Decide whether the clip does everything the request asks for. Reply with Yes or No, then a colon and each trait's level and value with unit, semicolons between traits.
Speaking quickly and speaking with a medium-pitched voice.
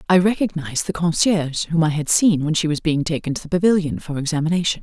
Yes: fast, 225 wpm; medium, 165 Hz